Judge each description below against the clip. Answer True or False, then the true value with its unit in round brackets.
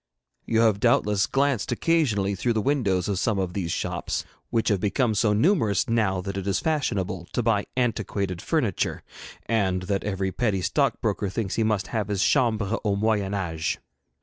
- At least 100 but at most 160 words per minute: False (175 wpm)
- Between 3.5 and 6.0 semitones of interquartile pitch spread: False (3.0 semitones)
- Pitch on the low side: True (105 Hz)